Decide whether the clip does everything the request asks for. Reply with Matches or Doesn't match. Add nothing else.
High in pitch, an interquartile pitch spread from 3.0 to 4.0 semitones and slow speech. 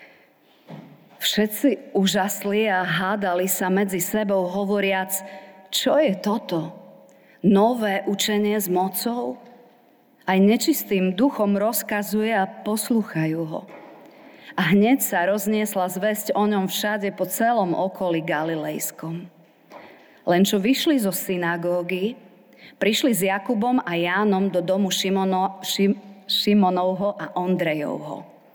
Doesn't match